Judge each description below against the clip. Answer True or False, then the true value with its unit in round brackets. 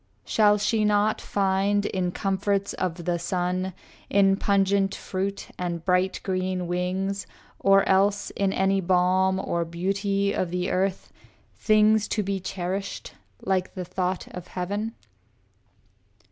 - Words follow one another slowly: True (130 wpm)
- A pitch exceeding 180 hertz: True (190 Hz)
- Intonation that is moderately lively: False (1.6 semitones)